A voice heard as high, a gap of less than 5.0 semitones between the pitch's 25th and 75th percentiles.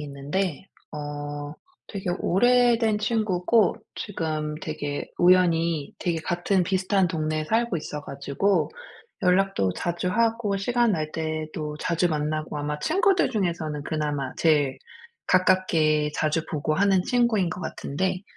No: medium, 170 Hz; average, 4.3 semitones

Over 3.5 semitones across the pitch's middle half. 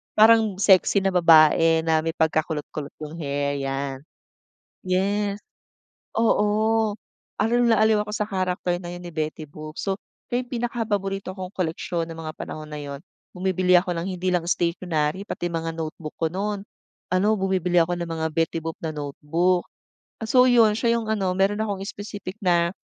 Yes: average, 4.1 semitones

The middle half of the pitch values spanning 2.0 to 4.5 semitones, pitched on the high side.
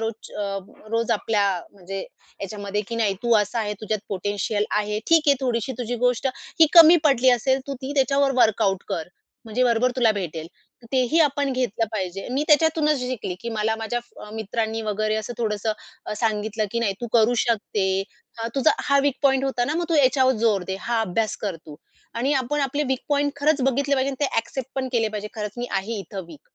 Yes: average, 4.1 semitones; high, 230 Hz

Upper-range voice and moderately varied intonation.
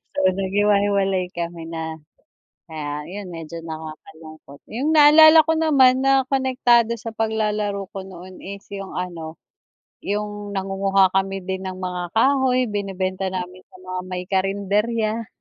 Yes: high, 195 Hz; average, 3.4 semitones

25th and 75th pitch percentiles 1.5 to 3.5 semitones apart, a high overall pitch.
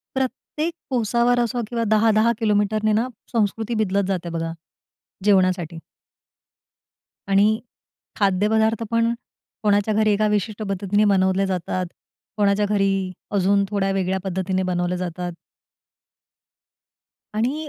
Yes: average, 2.7 semitones; high, 205 Hz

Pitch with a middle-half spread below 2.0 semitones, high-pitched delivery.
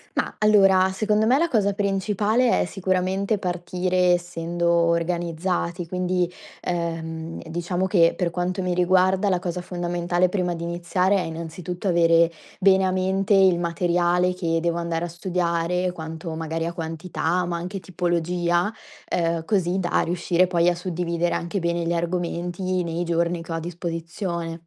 No: narrow, 1.6 semitones; medium, 175 Hz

